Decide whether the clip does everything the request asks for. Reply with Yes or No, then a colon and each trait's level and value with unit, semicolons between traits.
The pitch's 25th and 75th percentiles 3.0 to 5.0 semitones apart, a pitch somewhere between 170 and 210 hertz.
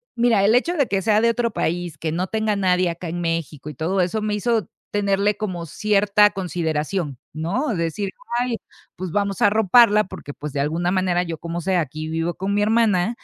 Yes: average, 4.0 semitones; high, 190 Hz